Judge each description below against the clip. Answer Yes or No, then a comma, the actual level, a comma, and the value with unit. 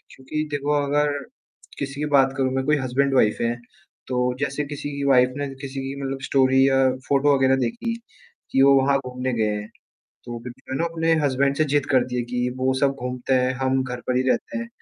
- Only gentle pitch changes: Yes, narrow, 1.8 semitones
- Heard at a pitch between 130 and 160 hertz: Yes, low, 135 Hz